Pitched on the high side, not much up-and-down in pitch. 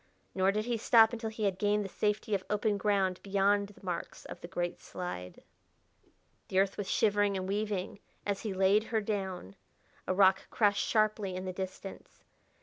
Yes: high, 200 Hz; narrow, 1.9 semitones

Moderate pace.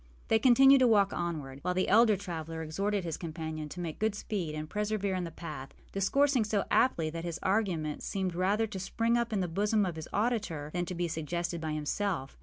No: fast, 210 wpm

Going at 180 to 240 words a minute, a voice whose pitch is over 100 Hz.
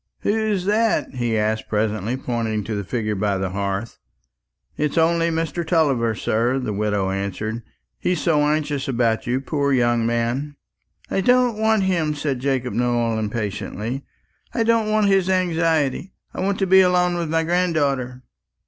No: average, 155 wpm; low, 135 Hz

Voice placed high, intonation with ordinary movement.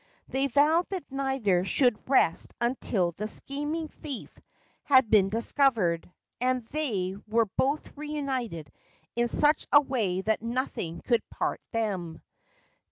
No: high, 240 Hz; wide, 5.7 semitones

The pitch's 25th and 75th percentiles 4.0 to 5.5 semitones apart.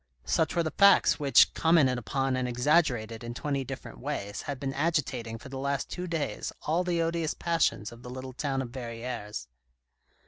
Yes: average, 4.6 semitones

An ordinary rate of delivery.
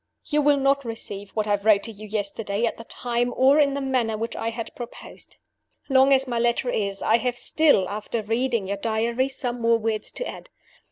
No: fast, 210 wpm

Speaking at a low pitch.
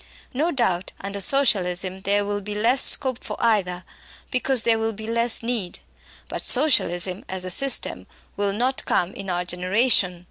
No: high, 205 Hz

